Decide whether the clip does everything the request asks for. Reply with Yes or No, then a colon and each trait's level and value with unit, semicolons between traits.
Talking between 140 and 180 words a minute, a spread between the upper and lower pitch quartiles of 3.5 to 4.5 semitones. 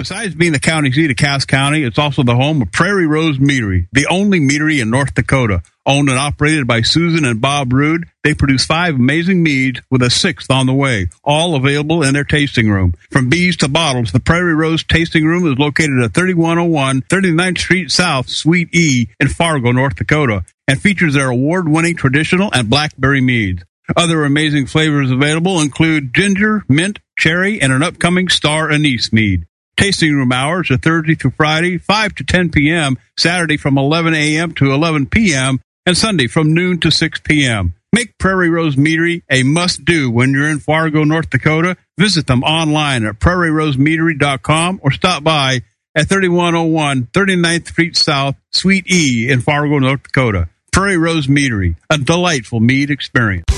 Yes: average, 175 wpm; average, 4.0 semitones